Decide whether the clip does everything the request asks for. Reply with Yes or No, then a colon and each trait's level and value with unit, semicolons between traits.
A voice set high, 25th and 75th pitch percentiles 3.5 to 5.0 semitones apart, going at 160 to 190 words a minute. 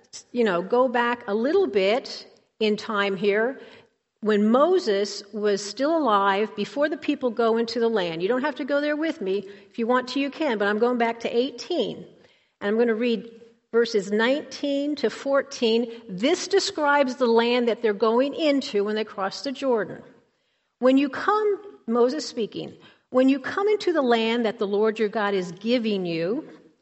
Yes: high, 235 Hz; average, 4.7 semitones; average, 185 wpm